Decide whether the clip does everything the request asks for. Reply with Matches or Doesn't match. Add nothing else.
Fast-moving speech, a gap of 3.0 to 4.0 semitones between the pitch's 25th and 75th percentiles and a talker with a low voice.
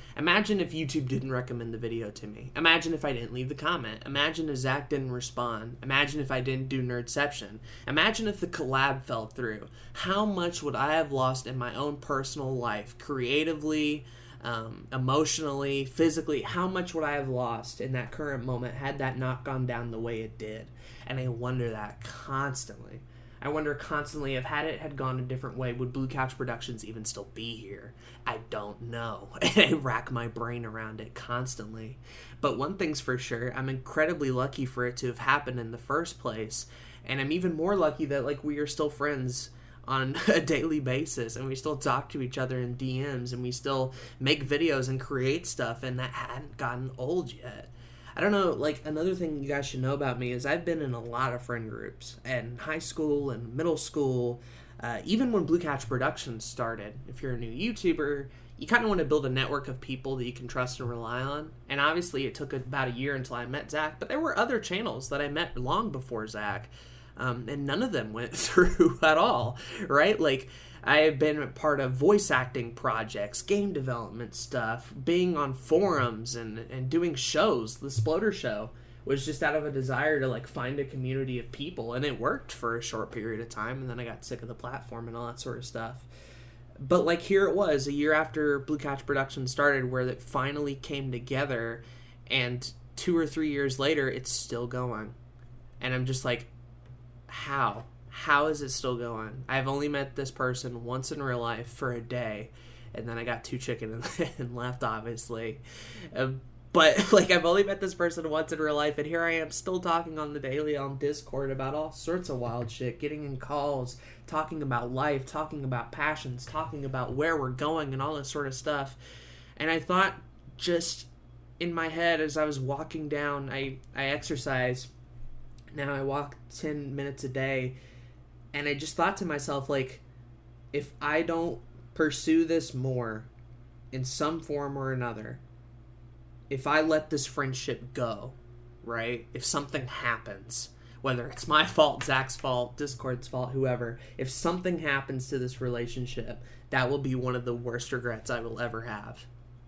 Doesn't match